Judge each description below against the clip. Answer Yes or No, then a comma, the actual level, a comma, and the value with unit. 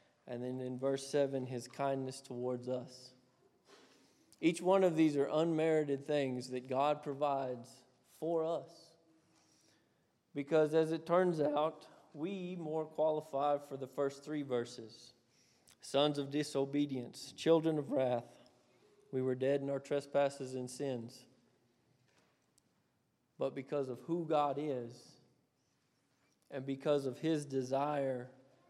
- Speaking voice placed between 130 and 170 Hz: Yes, medium, 140 Hz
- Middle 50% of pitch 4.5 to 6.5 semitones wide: No, average, 3.2 semitones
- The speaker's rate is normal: No, slow, 125 wpm